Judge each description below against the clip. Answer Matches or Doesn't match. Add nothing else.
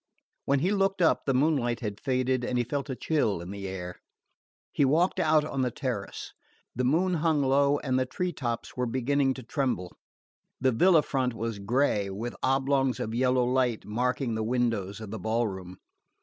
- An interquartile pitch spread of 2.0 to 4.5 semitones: Matches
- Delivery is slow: Doesn't match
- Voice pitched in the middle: Doesn't match